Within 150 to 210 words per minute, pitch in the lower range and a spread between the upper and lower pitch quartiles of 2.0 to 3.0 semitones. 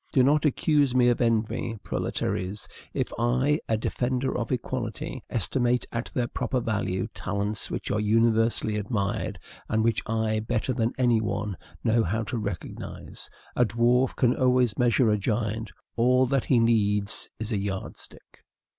Yes: average, 155 wpm; low, 115 Hz; narrow, 2.5 semitones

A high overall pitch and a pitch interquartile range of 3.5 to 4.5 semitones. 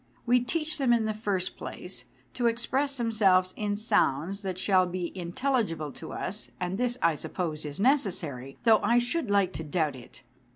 No: high, 200 Hz; wide, 5.4 semitones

